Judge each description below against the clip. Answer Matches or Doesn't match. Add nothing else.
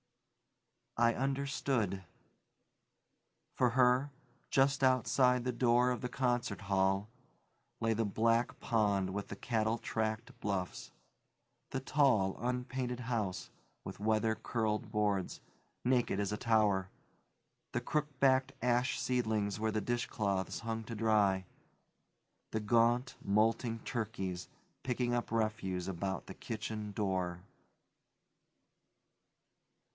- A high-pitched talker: Doesn't match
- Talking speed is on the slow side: Matches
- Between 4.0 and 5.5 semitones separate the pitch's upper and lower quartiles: Doesn't match